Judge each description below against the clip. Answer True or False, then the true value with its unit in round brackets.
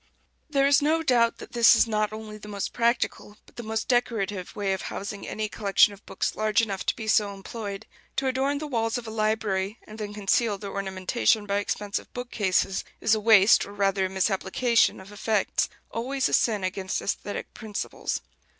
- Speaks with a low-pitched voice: False (215 Hz)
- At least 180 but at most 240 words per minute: True (190 wpm)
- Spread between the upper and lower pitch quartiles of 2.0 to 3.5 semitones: True (2.6 semitones)